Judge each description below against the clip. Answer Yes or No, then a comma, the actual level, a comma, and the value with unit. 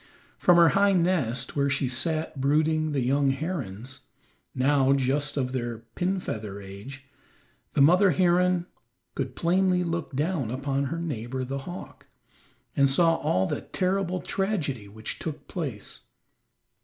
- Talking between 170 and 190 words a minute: No, average, 145 wpm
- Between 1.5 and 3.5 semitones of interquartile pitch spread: No, average, 5.0 semitones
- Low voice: No, medium, 145 Hz